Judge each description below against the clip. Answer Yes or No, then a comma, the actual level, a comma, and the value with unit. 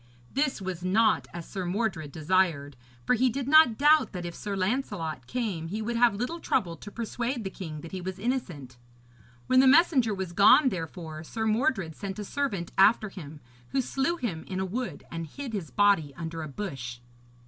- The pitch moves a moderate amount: No, wide, 6.4 semitones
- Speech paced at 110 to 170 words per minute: No, average, 190 wpm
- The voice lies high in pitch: Yes, high, 195 Hz